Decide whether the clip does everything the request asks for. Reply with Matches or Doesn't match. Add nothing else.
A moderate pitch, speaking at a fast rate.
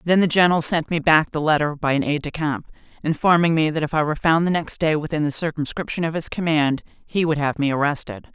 Matches